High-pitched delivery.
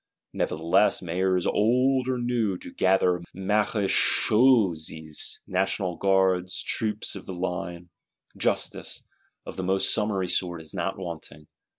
No: very low, 95 Hz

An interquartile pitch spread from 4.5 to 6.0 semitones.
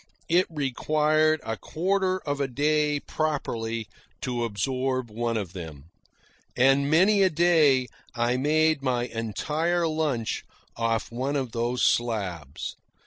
Yes: average, 5.1 semitones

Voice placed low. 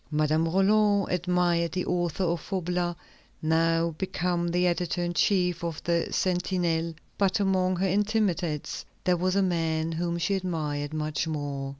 No: medium, 175 Hz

